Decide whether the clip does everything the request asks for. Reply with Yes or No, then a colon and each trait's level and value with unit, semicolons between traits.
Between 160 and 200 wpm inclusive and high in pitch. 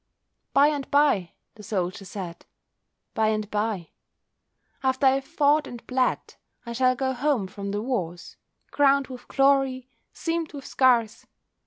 No: average, 140 wpm; very high, 255 Hz